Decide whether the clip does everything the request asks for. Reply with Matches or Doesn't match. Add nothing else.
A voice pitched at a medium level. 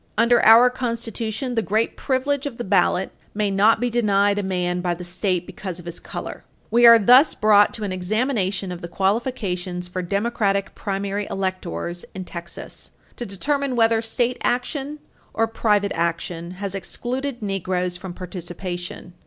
Doesn't match